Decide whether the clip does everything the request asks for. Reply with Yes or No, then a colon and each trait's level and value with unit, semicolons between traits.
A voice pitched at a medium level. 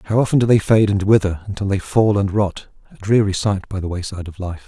No: low, 100 Hz